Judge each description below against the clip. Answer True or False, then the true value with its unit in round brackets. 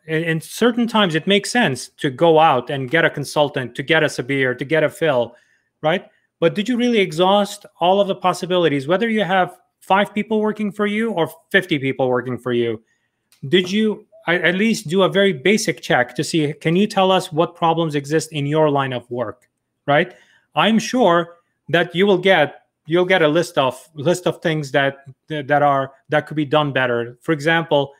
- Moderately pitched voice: True (165 Hz)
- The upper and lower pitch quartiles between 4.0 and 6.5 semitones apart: True (4.6 semitones)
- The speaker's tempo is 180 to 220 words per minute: True (200 wpm)